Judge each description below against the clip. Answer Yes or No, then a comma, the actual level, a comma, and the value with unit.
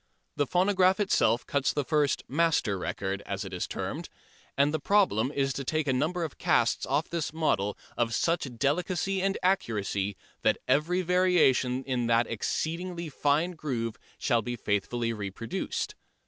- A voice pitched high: No, medium, 140 Hz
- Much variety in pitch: Yes, wide, 6.7 semitones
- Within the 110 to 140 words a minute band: No, average, 155 wpm